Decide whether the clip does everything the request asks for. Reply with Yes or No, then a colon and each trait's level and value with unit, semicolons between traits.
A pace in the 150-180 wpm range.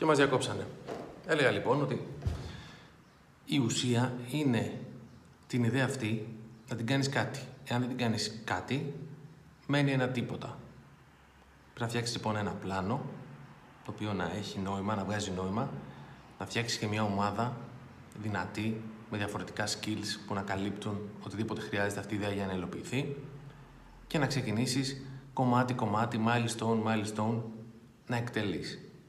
No: average, 135 wpm